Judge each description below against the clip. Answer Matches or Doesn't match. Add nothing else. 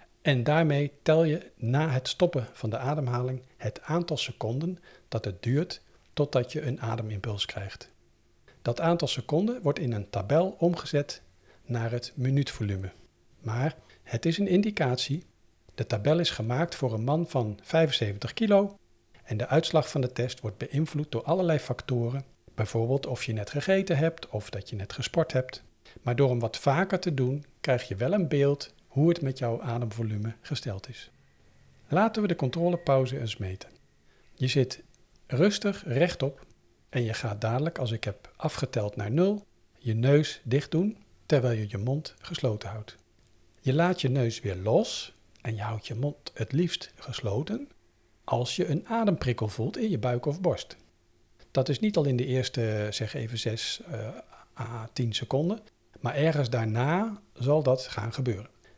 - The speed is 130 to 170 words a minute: Matches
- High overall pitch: Doesn't match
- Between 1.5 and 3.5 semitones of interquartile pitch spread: Doesn't match